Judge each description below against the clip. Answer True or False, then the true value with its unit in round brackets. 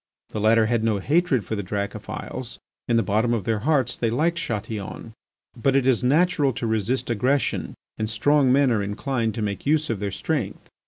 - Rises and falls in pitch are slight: False (4.1 semitones)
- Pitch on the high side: False (115 Hz)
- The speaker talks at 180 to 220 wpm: True (195 wpm)